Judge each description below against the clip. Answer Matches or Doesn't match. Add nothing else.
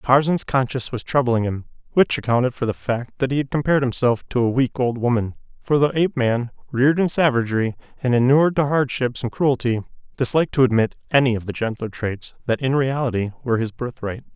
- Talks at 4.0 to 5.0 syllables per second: Doesn't match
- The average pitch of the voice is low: Matches